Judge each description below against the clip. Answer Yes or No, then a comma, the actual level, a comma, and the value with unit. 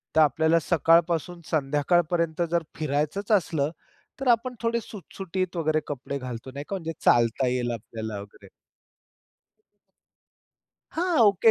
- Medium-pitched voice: Yes, medium, 160 Hz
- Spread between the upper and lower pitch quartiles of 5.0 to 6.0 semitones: No, average, 4.4 semitones